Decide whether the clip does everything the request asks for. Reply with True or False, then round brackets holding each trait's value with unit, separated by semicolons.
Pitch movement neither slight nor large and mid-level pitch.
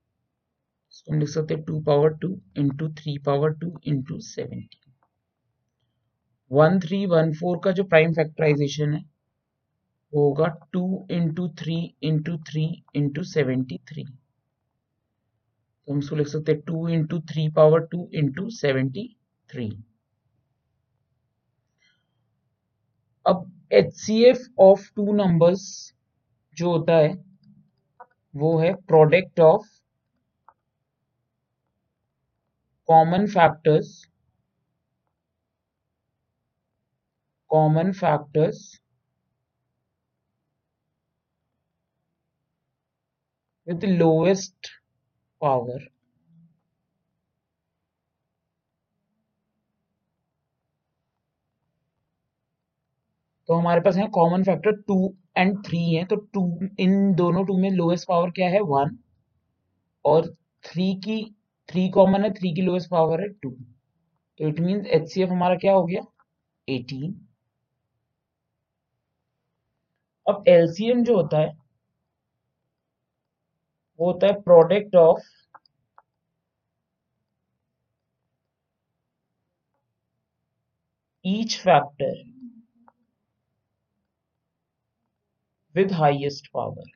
True (4.7 semitones; 160 Hz)